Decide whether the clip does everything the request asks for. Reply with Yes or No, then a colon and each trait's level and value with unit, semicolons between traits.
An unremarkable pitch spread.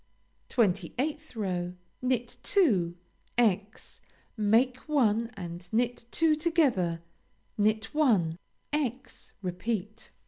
No: wide, 5.9 semitones